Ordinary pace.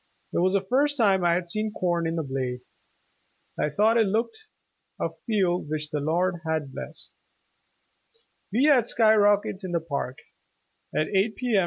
Yes: average, 175 wpm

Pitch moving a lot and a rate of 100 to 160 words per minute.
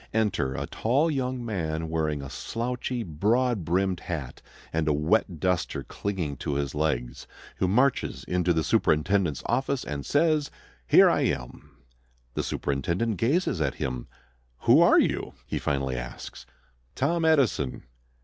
Yes: wide, 8.4 semitones; average, 140 wpm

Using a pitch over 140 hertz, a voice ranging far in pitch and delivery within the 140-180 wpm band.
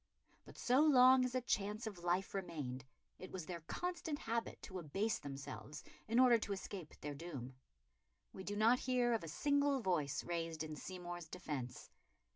Yes: high, 190 Hz; wide, 7.2 semitones; average, 170 wpm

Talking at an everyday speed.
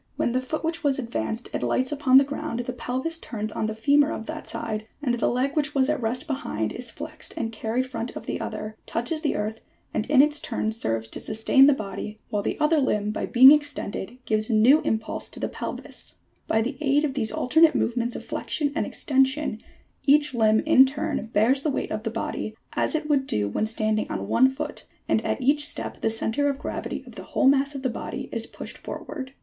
No: fast, 225 wpm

